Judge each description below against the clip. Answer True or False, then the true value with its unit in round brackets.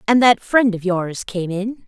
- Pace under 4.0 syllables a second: False (4.1 syllables/s)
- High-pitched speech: True (205 Hz)